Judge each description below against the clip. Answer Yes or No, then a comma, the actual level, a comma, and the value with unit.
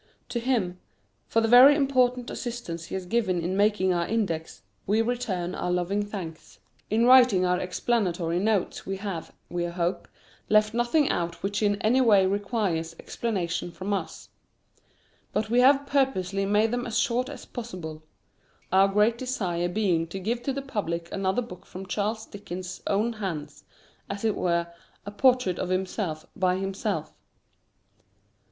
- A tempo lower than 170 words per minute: Yes, average, 155 wpm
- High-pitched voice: Yes, high, 200 Hz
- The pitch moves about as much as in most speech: Yes, average, 4.7 semitones